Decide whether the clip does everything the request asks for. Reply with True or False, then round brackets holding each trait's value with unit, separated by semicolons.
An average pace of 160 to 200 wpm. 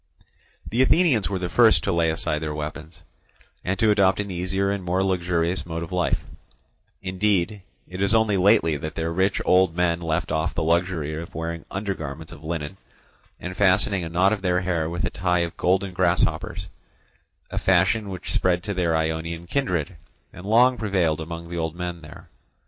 True (185 wpm)